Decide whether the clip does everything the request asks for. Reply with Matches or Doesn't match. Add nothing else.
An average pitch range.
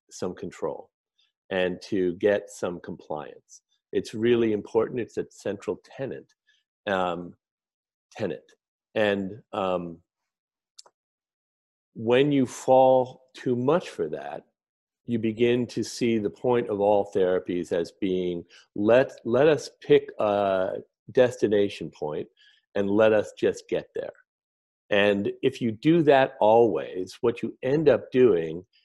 Doesn't match